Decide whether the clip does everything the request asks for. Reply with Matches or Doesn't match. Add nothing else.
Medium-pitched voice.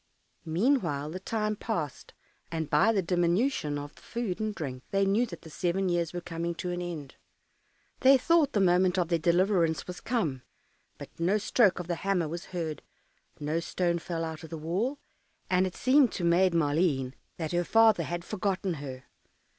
Matches